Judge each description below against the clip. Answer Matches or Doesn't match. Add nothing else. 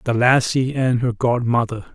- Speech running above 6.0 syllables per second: Doesn't match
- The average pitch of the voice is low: Matches